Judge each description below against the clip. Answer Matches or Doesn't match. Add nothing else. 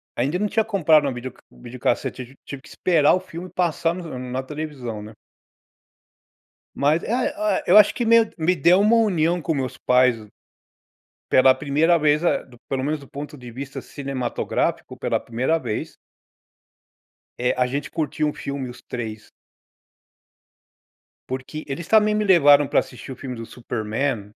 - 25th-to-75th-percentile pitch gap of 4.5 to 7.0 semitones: Matches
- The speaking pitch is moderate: Matches